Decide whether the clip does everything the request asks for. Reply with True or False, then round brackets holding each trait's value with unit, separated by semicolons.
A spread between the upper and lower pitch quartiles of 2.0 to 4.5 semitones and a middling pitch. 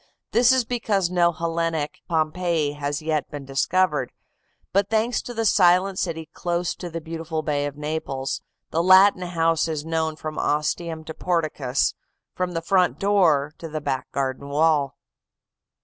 True (3.1 semitones; 165 Hz)